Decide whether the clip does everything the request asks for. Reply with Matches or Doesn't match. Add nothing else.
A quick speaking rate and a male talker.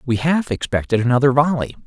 Doesn't match